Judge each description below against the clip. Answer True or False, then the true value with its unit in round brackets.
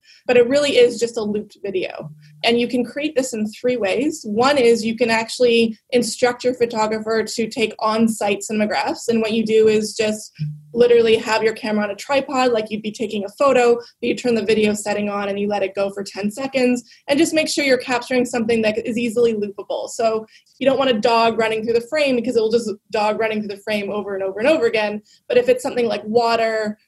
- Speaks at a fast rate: True (235 wpm)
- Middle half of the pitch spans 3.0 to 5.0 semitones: False (2.5 semitones)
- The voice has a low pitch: False (225 Hz)